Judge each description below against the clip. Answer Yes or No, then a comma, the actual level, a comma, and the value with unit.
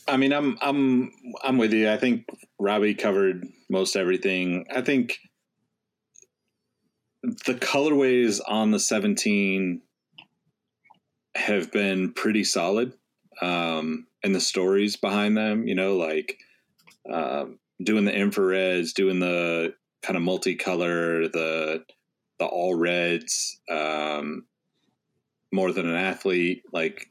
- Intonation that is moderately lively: No, wide, 6.0 semitones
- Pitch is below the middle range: Yes, very low, 95 Hz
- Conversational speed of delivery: No, slow, 115 wpm